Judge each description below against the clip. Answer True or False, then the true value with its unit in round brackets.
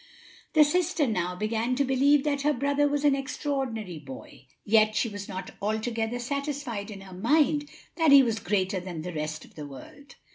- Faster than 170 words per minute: True (185 wpm)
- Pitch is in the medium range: False (230 Hz)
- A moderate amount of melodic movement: False (6.6 semitones)